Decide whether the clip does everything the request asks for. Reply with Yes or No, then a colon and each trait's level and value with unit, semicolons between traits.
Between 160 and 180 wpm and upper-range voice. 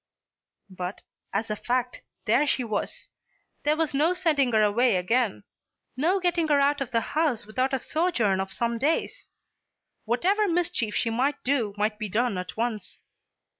Yes: average, 165 wpm; high, 245 Hz